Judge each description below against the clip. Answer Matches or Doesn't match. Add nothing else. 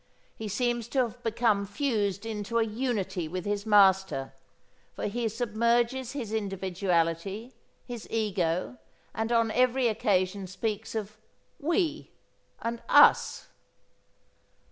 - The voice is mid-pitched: Doesn't match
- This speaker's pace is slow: Matches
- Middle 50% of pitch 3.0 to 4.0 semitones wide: Matches